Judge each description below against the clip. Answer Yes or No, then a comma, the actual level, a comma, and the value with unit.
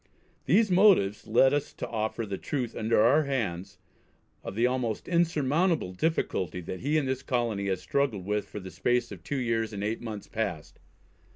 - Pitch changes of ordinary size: No, wide, 5.8 semitones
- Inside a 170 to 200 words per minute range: Yes, average, 180 wpm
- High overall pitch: No, low, 115 Hz